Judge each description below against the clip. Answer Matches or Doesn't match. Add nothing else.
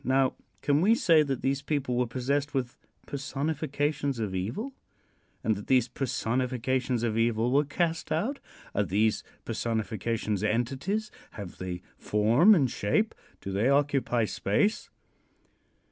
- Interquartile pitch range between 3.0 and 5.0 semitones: Matches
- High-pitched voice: Doesn't match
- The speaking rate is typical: Doesn't match